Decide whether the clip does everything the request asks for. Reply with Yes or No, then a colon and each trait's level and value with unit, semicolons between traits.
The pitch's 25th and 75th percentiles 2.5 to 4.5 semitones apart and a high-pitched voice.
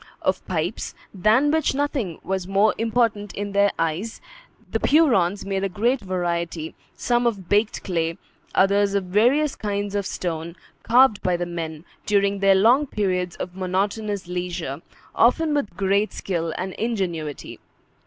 Yes: average, 3.6 semitones; high, 195 Hz